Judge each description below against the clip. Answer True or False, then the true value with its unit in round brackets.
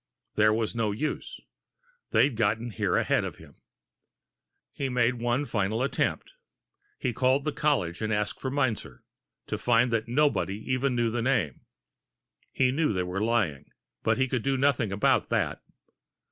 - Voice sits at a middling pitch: False (120 Hz)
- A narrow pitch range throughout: False (3.6 semitones)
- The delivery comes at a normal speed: True (155 wpm)